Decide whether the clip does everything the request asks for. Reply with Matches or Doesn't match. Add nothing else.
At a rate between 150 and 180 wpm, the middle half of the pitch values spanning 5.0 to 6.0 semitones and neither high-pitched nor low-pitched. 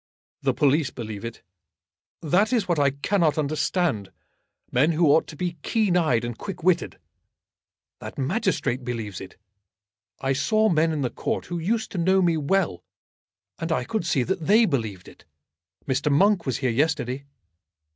Matches